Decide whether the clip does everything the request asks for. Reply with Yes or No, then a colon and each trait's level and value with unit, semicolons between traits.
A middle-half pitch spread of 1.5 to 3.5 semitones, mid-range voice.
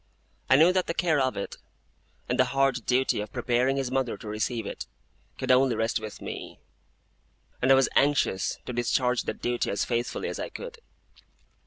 No: narrow, 2.4 semitones; low, 125 Hz